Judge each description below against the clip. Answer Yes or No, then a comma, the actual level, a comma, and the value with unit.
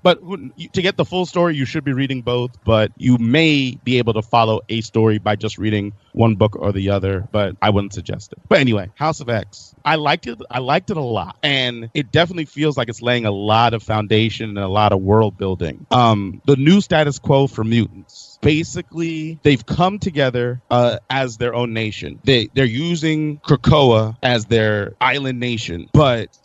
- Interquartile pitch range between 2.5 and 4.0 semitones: No, average, 5.2 semitones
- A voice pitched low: Yes, low, 120 Hz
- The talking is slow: No, average, 200 wpm